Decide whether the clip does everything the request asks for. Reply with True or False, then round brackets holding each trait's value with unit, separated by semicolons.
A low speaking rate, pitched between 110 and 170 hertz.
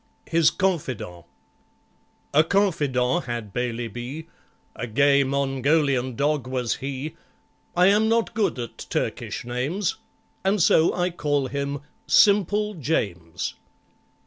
True (115 wpm; 140 Hz)